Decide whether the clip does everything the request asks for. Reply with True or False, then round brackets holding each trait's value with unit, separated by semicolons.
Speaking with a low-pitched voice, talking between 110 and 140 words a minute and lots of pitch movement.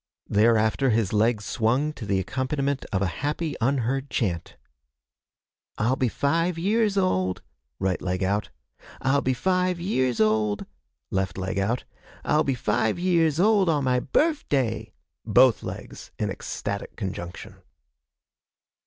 True (125 Hz; 135 wpm; 6.5 semitones)